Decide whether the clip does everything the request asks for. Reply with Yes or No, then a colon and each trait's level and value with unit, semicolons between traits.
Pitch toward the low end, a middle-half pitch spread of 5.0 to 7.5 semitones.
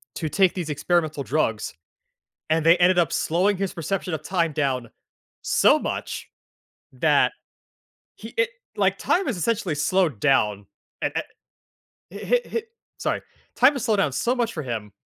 No: medium, 165 Hz; average, 5.3 semitones